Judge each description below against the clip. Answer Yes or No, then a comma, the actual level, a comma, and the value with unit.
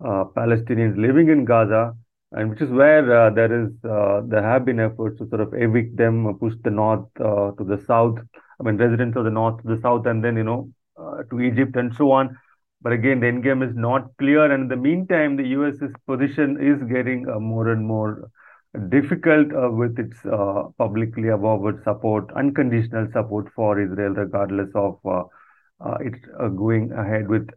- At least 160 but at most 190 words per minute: No, average, 200 wpm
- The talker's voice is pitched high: No, low, 115 Hz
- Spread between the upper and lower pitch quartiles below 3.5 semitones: Yes, average, 2.9 semitones